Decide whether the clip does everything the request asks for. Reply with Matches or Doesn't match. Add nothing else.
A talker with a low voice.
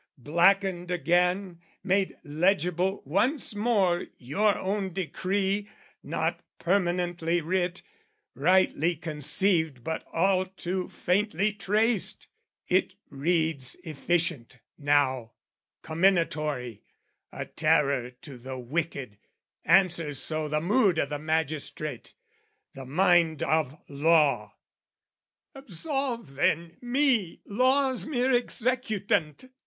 Doesn't match